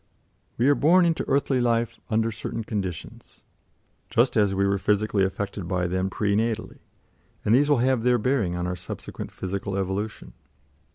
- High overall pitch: No, low, 105 Hz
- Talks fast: No, average, 165 wpm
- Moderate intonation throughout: Yes, average, 3.9 semitones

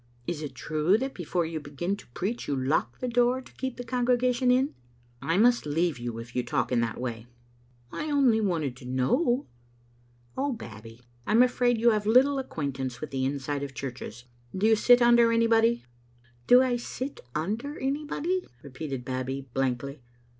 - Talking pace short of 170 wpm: No, average, 190 wpm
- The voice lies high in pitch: No, medium, 175 Hz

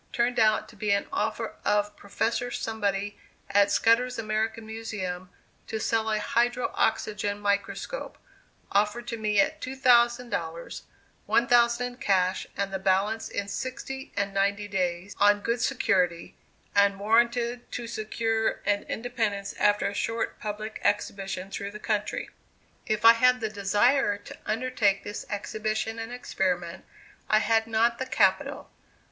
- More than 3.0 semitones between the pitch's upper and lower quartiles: No, average, 2.7 semitones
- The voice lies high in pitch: Yes, high, 215 Hz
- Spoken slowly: No, average, 145 wpm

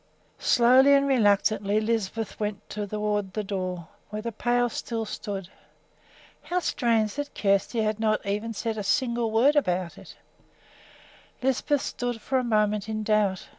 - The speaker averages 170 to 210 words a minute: No, average, 150 wpm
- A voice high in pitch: Yes, high, 215 Hz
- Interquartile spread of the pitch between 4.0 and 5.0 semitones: No, average, 2.7 semitones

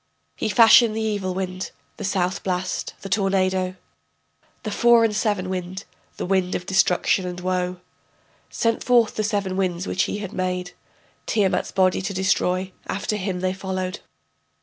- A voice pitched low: No, high, 190 Hz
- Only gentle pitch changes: Yes, narrow, 1.9 semitones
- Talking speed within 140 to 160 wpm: Yes, average, 155 wpm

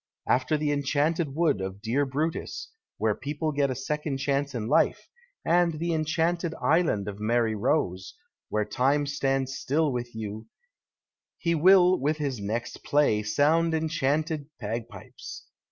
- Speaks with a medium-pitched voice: Yes, medium, 145 Hz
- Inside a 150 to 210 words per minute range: No, average, 140 wpm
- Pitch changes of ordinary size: Yes, average, 4.7 semitones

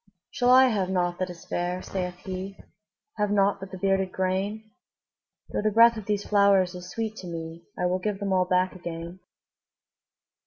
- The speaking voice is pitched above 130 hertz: Yes, high, 190 Hz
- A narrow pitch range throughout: Yes, narrow, 2.3 semitones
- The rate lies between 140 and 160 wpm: No, average, 185 wpm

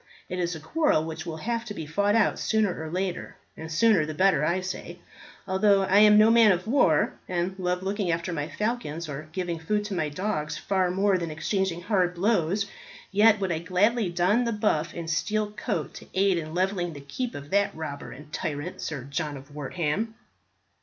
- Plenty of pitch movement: No, average, 4.5 semitones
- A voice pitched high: No, medium, 180 Hz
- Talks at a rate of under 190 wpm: No, fast, 205 wpm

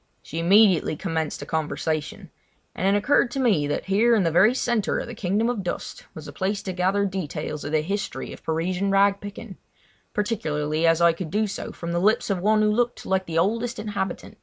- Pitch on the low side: No, high, 195 Hz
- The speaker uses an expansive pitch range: No, average, 4.1 semitones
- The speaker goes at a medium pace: No, fast, 210 wpm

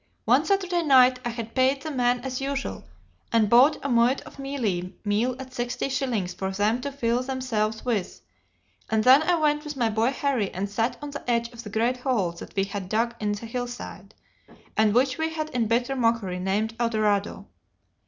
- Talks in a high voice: Yes, high, 240 Hz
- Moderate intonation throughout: Yes, average, 3.8 semitones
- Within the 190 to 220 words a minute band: Yes, average, 200 wpm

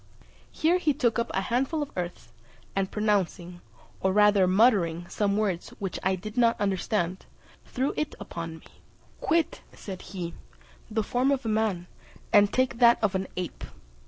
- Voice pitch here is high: Yes, high, 205 Hz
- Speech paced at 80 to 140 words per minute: No, average, 160 wpm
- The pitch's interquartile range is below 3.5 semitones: No, average, 4.3 semitones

